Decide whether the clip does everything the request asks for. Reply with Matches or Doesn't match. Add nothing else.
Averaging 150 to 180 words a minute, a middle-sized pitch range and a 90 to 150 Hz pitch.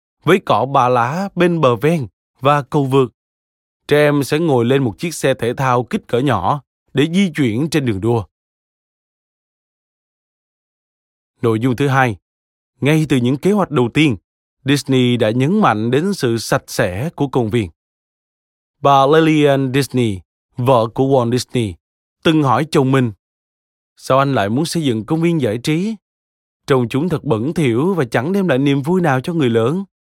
Matches